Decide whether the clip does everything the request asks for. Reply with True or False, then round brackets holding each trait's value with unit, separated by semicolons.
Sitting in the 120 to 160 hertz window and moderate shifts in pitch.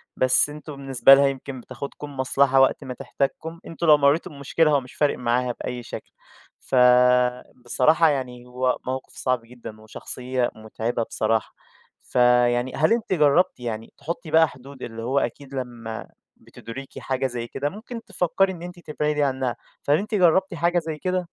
True (135 Hz; 3.7 semitones)